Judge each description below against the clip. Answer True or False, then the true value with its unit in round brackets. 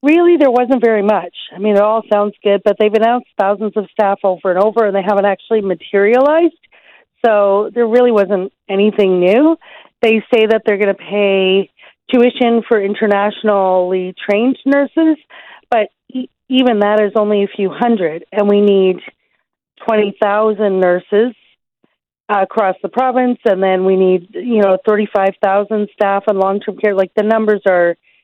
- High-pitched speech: True (210 Hz)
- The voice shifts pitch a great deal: False (2.7 semitones)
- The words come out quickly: False (160 wpm)